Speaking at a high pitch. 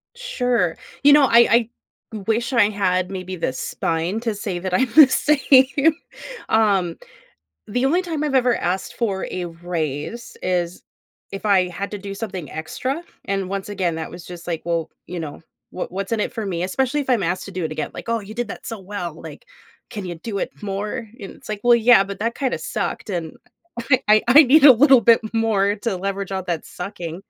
Yes: high, 200 Hz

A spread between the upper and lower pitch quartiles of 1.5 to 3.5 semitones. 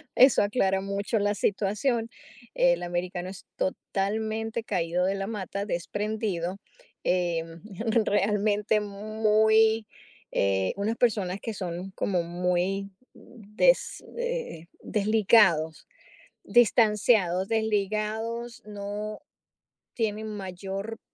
Yes: average, 2.8 semitones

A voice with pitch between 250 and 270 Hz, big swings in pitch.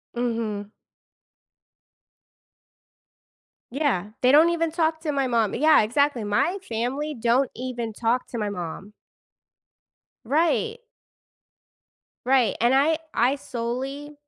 No: very high, 255 Hz; average, 4.4 semitones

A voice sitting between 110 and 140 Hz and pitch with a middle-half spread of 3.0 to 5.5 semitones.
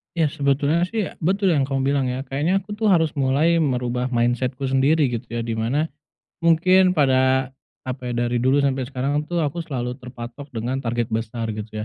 Yes: low, 135 Hz; average, 4.1 semitones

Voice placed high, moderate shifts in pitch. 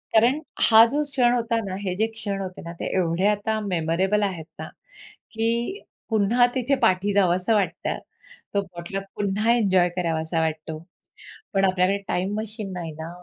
Yes: high, 195 Hz; average, 3.8 semitones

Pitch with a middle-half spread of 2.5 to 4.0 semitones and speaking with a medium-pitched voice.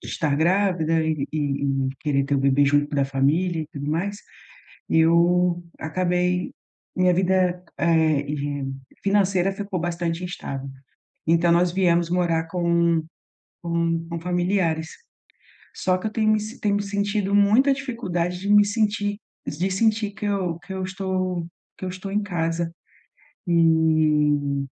Yes: average, 3.2 semitones; medium, 175 Hz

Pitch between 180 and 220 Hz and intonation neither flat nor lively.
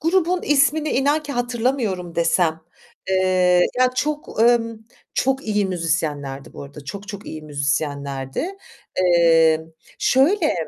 No: high, 190 Hz; wide, 8.9 semitones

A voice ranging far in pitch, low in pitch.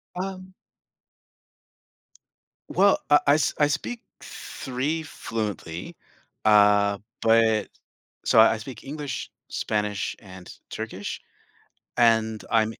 Yes: wide, 5.8 semitones; low, 115 Hz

